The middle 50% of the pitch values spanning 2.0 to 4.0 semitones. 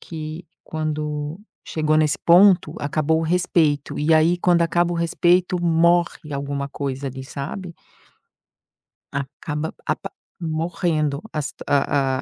Yes: average, 2.9 semitones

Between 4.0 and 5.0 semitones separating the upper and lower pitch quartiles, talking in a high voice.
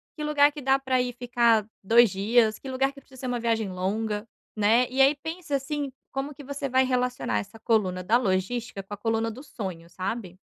Yes: average, 4.3 semitones; high, 240 Hz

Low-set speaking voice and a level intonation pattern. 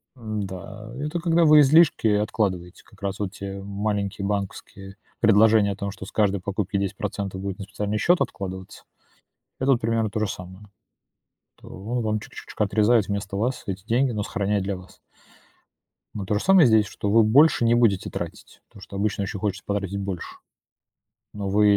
Yes: low, 105 Hz; narrow, 2.2 semitones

